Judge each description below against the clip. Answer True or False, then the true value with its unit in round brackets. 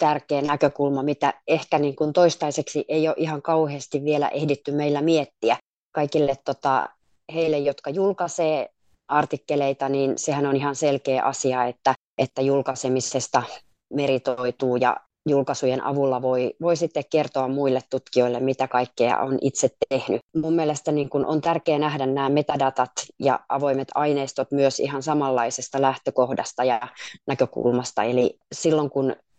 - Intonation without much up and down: True (2.2 semitones)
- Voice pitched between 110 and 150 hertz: True (140 Hz)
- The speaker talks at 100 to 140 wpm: True (135 wpm)